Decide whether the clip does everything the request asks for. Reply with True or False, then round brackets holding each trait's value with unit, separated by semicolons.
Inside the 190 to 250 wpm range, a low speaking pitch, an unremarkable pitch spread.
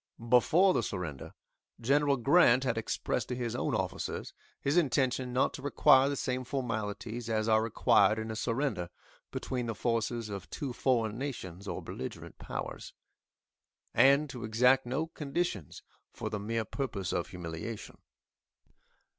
False (145 wpm; 120 Hz; 3.5 semitones)